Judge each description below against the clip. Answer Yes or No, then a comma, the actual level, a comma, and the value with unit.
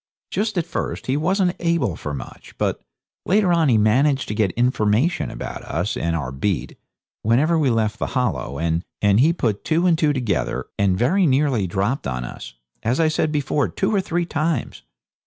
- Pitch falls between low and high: No, low, 130 Hz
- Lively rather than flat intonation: Yes, wide, 8.1 semitones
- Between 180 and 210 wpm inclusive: Yes, average, 185 wpm